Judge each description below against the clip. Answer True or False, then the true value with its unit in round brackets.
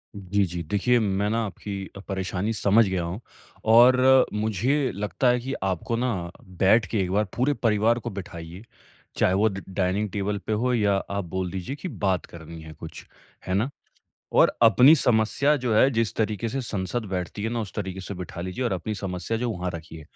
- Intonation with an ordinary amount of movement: True (3.8 semitones)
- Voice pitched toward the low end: True (100 Hz)